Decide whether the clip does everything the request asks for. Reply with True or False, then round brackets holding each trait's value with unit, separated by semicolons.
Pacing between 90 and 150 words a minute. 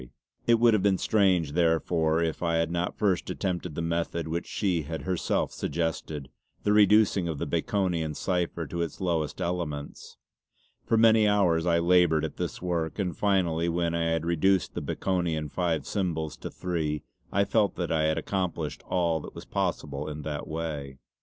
False (170 wpm)